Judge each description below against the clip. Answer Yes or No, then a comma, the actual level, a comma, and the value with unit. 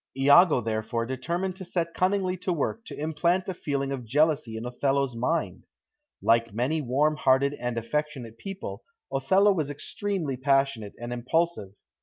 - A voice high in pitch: No, medium, 140 Hz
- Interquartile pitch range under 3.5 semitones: No, wide, 5.5 semitones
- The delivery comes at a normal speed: Yes, average, 150 wpm